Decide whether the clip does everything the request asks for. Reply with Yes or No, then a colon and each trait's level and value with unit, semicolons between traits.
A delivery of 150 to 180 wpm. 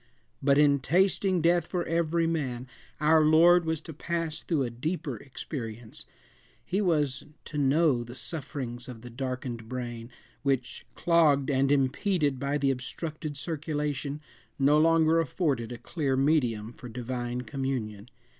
No: average, 140 wpm